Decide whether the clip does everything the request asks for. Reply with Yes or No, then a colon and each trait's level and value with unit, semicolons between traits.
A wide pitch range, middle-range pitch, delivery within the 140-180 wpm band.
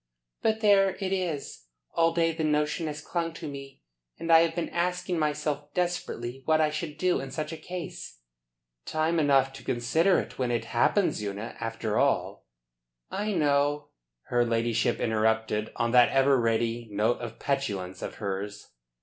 Yes: wide, 6.1 semitones; medium, 145 Hz; average, 165 wpm